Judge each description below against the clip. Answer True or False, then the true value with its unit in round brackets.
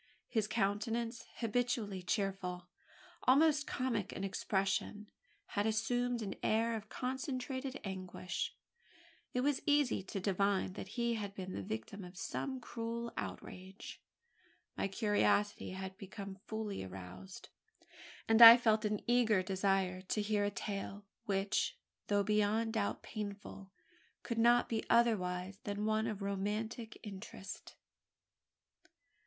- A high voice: True (210 Hz)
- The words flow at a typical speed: False (125 wpm)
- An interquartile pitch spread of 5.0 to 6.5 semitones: False (3.1 semitones)